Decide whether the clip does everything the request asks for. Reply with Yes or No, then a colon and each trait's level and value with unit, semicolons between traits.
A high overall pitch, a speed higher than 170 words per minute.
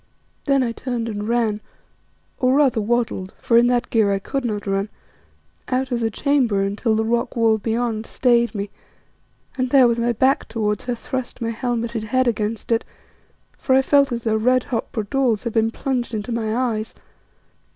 Yes: high, 235 Hz; average, 180 wpm